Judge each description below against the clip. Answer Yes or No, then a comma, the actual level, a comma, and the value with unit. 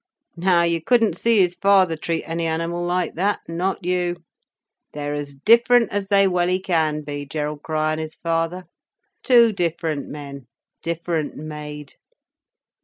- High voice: No, medium, 170 Hz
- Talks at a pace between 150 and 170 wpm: No, slow, 135 wpm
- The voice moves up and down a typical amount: Yes, average, 3.2 semitones